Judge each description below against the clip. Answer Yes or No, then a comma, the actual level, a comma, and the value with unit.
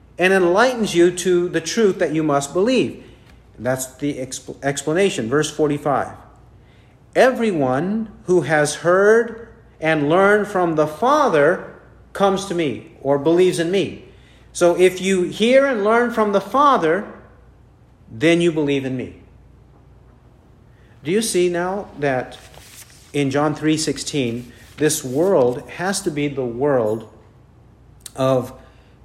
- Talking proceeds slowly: Yes, slow, 130 wpm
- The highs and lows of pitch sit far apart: Yes, wide, 6.4 semitones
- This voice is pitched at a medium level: Yes, medium, 150 Hz